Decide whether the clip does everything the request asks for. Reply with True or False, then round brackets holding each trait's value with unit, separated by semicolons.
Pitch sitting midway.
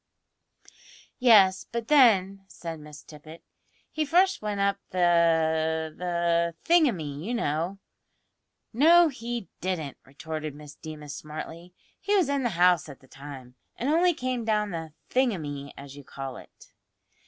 True (175 Hz)